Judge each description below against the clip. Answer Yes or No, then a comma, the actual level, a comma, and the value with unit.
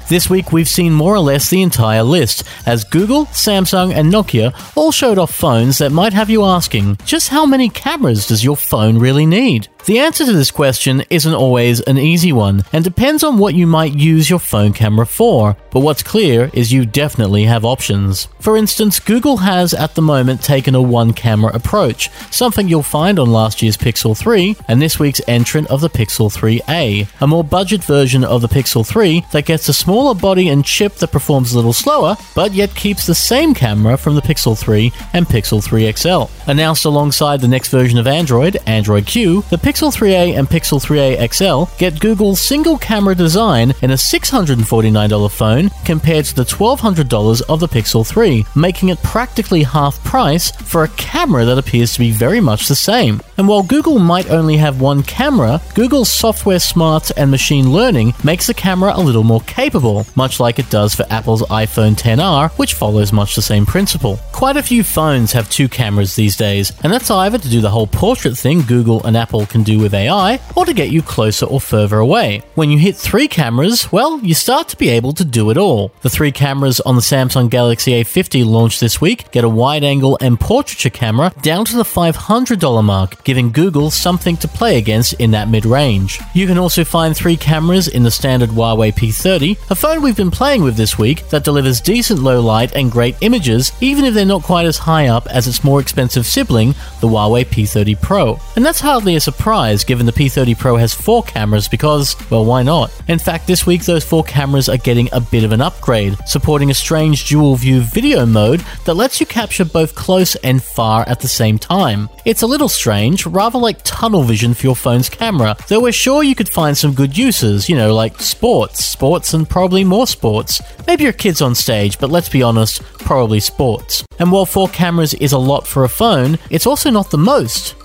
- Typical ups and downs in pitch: No, wide, 7.6 semitones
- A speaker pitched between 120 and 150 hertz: Yes, medium, 140 Hz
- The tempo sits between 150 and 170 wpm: No, fast, 205 wpm